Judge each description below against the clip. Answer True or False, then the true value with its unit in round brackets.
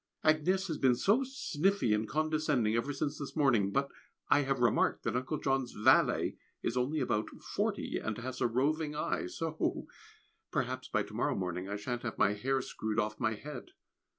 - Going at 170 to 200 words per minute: True (180 wpm)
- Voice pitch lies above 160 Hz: False (135 Hz)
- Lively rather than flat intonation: True (5.7 semitones)